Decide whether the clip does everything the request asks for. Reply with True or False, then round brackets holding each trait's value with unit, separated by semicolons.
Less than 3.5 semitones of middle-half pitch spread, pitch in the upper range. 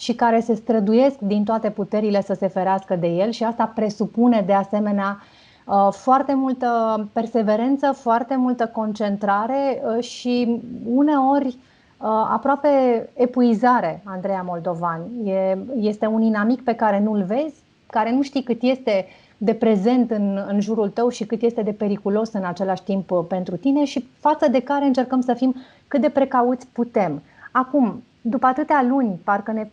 False (3.8 semitones; 230 Hz)